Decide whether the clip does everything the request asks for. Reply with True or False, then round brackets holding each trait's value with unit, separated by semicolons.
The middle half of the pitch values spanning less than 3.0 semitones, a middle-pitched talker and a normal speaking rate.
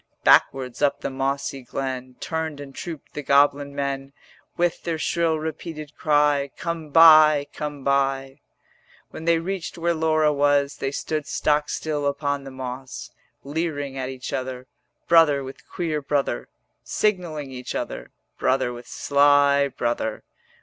True (2.5 semitones; 145 Hz; 145 wpm)